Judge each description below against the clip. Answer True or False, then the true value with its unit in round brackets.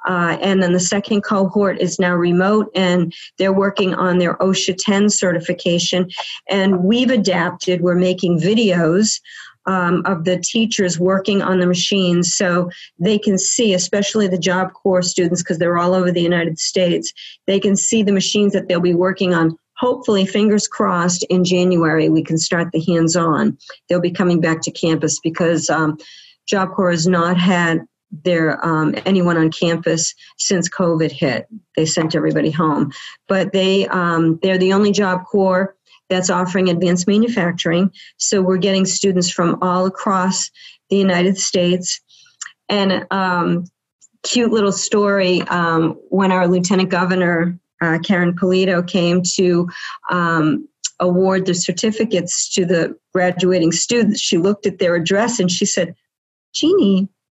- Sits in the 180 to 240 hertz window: True (185 Hz)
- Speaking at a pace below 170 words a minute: True (155 wpm)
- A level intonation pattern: True (2.0 semitones)